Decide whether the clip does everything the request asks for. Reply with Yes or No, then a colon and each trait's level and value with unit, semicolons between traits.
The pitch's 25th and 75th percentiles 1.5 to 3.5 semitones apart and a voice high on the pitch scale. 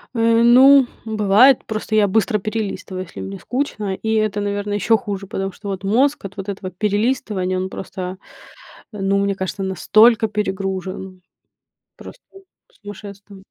Yes: narrow, 2.4 semitones; high, 205 Hz